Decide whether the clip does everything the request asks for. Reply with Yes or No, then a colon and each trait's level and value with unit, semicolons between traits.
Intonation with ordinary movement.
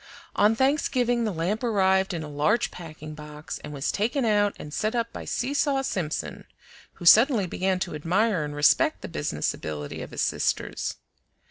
No: wide, 7.1 semitones